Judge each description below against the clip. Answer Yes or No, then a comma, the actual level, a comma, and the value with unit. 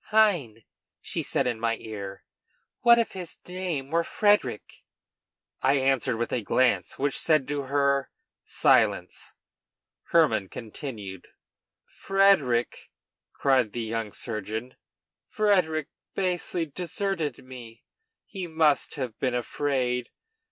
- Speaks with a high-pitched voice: No, low, 135 Hz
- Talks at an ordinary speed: No, slow, 110 wpm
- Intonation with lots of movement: Yes, wide, 6.2 semitones